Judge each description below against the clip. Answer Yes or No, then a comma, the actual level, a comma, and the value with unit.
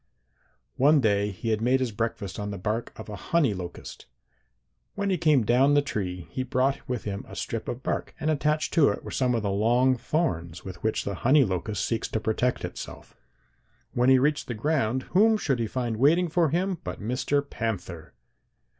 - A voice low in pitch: Yes, low, 125 Hz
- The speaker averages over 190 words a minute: Yes, average, 200 wpm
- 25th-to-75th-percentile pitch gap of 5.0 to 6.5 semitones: Yes, average, 5.3 semitones